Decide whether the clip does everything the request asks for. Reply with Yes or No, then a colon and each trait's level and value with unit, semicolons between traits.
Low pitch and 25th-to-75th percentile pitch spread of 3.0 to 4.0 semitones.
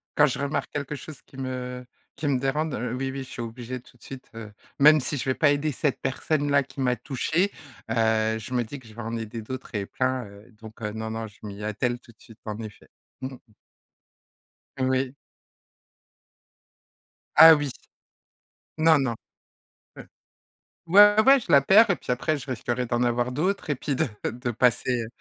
Yes: low, 130 Hz; average, 3.6 semitones